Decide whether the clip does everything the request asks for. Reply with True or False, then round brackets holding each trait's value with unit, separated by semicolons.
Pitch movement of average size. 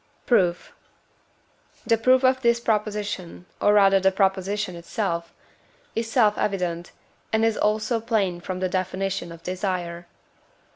True (3.3 semitones)